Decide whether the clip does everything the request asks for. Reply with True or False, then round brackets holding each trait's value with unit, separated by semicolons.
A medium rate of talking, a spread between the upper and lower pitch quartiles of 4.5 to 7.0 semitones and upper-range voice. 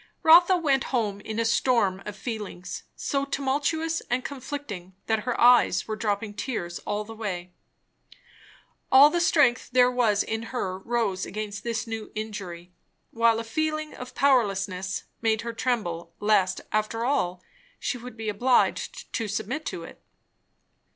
False (150 wpm; 4.0 semitones; 225 Hz)